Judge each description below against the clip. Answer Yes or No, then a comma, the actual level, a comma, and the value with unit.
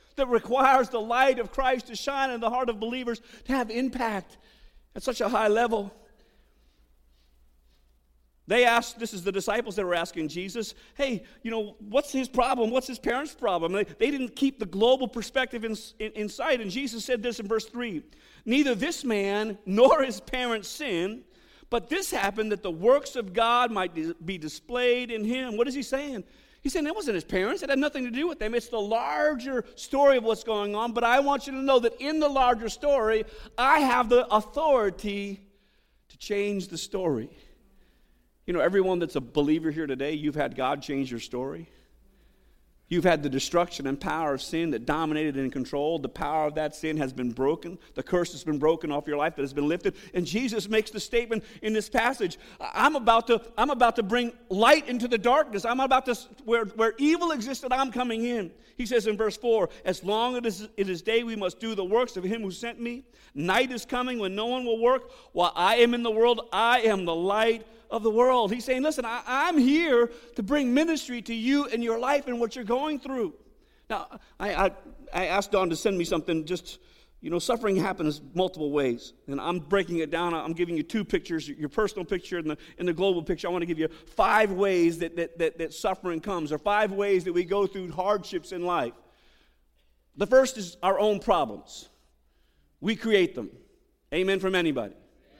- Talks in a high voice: Yes, high, 220 Hz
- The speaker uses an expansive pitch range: Yes, wide, 5.7 semitones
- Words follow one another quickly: Yes, fast, 210 wpm